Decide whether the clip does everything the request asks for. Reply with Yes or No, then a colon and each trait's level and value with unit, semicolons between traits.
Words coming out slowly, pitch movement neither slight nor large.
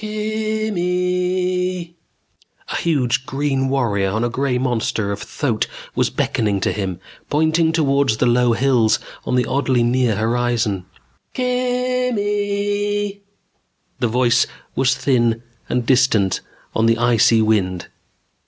No: slow, 125 wpm; wide, 7.7 semitones